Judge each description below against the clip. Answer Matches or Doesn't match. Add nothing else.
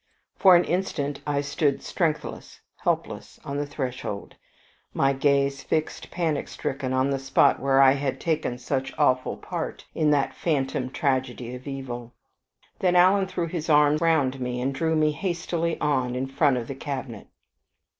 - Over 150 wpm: Matches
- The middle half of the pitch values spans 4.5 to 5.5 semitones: Doesn't match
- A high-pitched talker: Doesn't match